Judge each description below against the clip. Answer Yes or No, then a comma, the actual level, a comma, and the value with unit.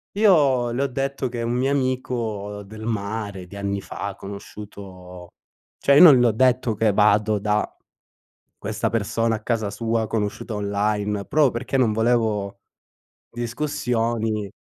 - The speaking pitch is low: Yes, low, 110 Hz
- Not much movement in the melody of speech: No, average, 3.2 semitones